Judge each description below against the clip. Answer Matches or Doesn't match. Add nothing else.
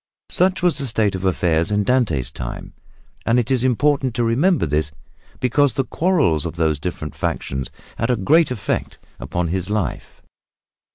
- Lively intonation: Matches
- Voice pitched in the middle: Doesn't match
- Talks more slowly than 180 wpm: Matches